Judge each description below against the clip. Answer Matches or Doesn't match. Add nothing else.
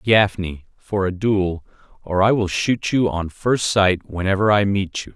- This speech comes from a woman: Doesn't match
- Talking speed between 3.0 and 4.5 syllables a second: Matches